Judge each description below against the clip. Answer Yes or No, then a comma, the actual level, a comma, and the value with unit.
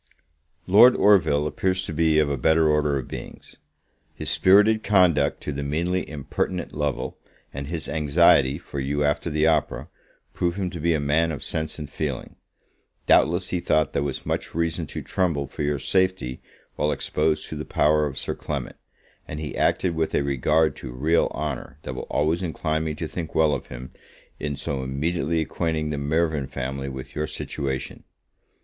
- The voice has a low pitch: Yes, very low, 75 Hz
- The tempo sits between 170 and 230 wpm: Yes, average, 180 wpm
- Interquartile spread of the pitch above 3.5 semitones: No, average, 2.7 semitones